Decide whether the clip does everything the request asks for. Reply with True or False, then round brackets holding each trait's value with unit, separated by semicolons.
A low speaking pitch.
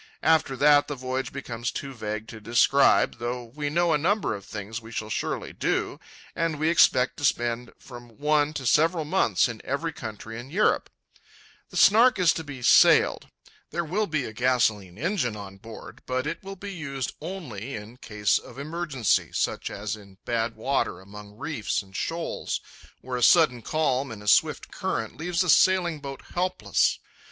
True (130 Hz)